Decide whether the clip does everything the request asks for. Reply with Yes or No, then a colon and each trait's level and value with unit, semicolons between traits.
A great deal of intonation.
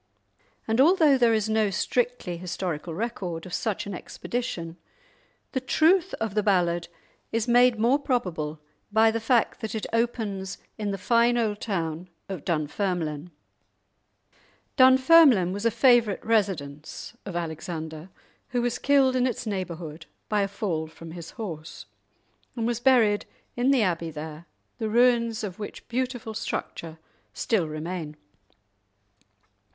Yes: wide, 5.9 semitones